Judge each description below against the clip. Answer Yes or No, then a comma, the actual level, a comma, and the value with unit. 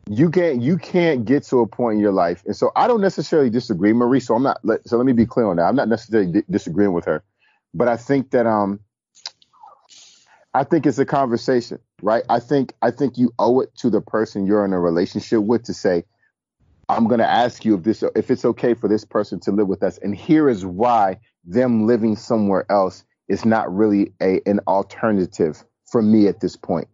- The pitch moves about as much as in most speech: Yes, average, 3.9 semitones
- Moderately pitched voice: No, low, 115 Hz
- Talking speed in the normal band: No, fast, 220 wpm